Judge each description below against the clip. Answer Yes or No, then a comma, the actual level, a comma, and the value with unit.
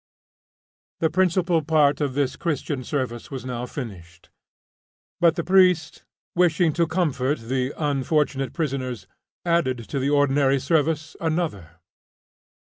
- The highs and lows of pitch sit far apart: No, average, 4.0 semitones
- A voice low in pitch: No, medium, 145 Hz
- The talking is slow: Yes, slow, 120 wpm